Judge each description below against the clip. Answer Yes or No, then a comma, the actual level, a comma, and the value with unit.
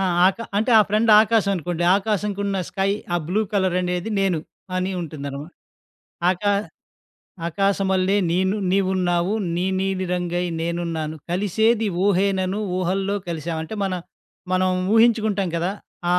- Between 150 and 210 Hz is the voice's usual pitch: Yes, high, 190 Hz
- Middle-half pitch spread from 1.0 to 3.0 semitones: Yes, narrow, 2.4 semitones